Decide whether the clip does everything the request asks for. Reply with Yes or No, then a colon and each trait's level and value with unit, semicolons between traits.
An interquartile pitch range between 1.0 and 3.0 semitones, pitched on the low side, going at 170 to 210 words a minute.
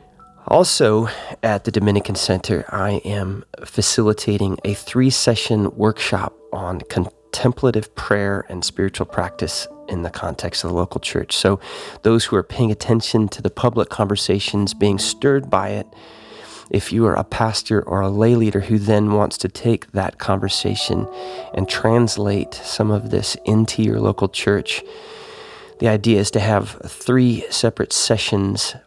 No: narrow, 2.5 semitones; low, 105 Hz; average, 150 wpm